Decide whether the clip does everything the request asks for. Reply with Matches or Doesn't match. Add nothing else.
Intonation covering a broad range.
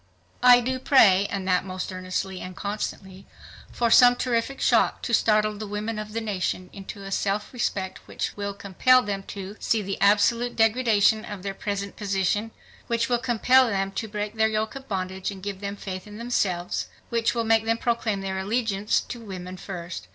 Doesn't match